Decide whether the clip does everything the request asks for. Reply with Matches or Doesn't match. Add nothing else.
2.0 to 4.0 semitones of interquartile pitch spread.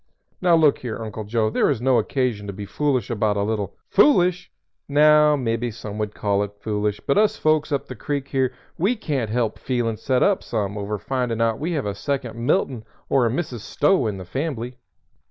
Doesn't match